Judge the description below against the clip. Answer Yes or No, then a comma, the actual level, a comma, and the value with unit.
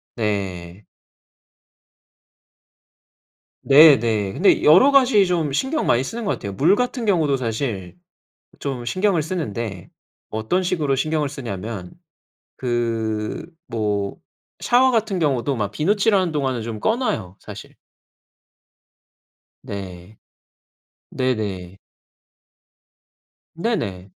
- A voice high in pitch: No, low, 130 Hz